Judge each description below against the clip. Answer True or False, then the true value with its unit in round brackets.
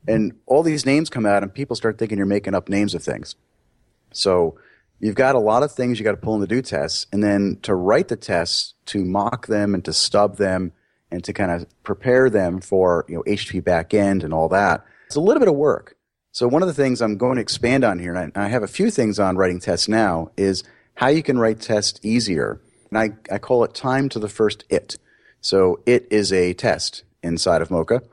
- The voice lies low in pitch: True (105 Hz)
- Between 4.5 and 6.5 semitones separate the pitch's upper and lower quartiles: False (3.8 semitones)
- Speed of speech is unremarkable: False (235 wpm)